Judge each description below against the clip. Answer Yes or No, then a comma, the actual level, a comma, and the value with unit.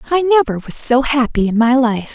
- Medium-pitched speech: No, very high, 255 Hz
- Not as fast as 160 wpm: No, fast, 225 wpm